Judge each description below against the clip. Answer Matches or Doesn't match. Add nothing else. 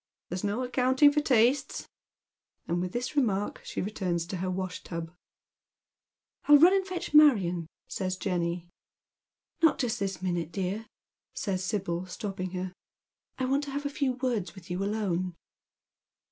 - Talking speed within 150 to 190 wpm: Matches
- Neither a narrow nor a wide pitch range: Doesn't match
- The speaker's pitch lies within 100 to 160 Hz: Doesn't match